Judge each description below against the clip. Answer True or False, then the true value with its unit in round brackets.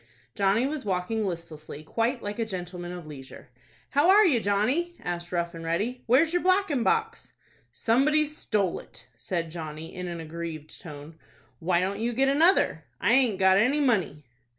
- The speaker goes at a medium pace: True (170 wpm)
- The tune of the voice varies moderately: False (7.9 semitones)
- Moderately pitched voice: False (200 Hz)